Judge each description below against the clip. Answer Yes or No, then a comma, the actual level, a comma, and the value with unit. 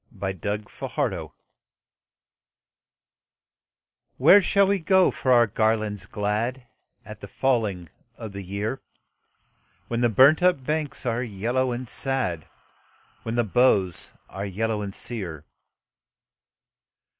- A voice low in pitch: Yes, low, 115 Hz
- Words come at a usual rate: No, slow, 120 wpm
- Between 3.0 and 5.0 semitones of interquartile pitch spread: Yes, average, 4.3 semitones